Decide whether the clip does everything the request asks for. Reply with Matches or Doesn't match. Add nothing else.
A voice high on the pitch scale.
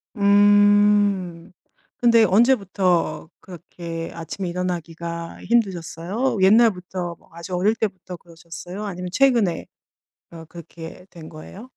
Doesn't match